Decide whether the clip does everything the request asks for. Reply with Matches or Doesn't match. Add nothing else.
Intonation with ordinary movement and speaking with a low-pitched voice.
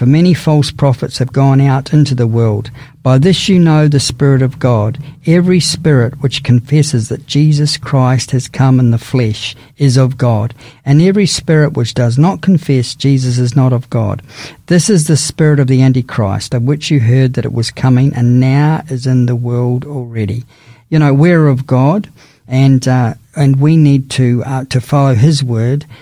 Matches